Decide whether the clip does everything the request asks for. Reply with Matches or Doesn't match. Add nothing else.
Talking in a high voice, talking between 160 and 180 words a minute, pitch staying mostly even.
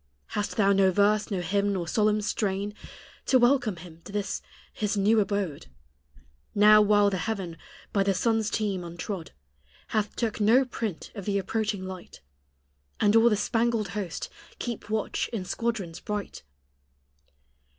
Doesn't match